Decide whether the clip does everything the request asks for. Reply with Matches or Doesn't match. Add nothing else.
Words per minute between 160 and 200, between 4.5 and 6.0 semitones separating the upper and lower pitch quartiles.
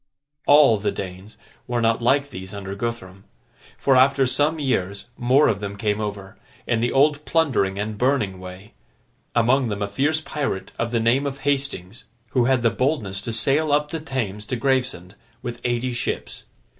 Matches